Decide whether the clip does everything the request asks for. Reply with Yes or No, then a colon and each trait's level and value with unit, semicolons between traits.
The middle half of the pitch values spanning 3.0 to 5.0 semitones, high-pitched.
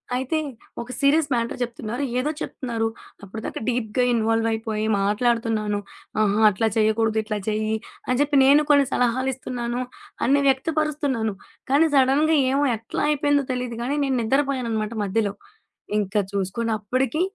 Yes: average, 3.7 semitones; high, 240 Hz